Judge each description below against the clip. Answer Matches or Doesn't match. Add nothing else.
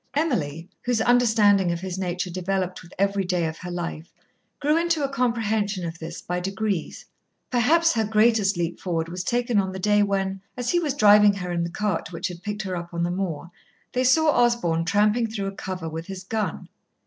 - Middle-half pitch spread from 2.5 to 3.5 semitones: Doesn't match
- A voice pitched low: Doesn't match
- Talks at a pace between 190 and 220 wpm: Matches